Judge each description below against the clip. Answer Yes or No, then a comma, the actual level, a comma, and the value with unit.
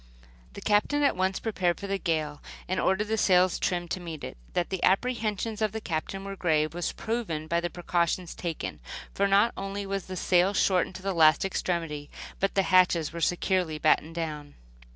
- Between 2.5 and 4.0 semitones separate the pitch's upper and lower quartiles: Yes, average, 3.0 semitones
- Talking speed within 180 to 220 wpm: Yes, average, 190 wpm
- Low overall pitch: No, medium, 185 Hz